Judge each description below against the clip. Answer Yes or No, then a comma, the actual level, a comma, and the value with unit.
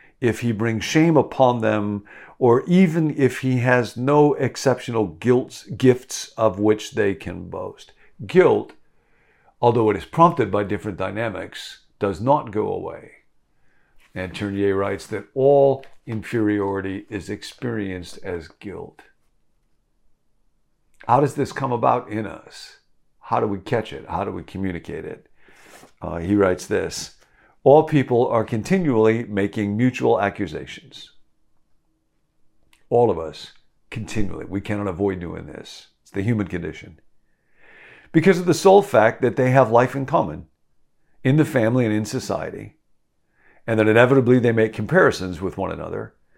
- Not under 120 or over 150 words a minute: Yes, average, 140 wpm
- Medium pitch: No, low, 110 Hz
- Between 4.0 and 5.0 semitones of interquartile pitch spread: Yes, average, 4.6 semitones